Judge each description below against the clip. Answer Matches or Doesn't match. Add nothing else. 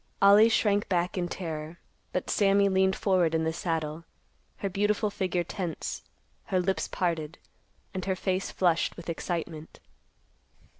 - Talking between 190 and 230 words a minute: Doesn't match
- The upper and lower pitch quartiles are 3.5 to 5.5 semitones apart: Doesn't match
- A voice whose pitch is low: Doesn't match